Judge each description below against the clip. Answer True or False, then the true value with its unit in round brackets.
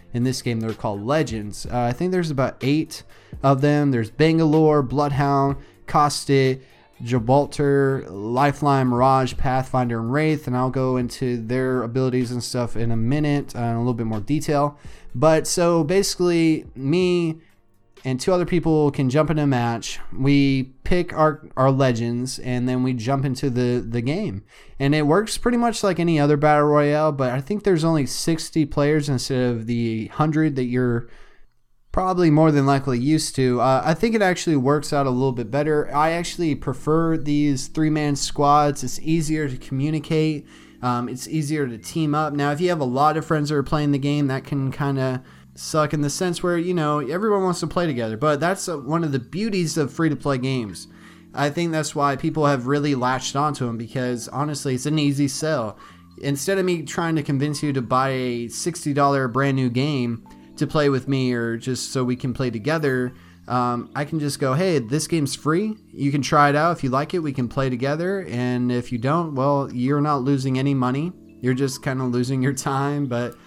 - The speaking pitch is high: False (140 Hz)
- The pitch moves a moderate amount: True (3.4 semitones)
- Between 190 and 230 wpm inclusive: True (200 wpm)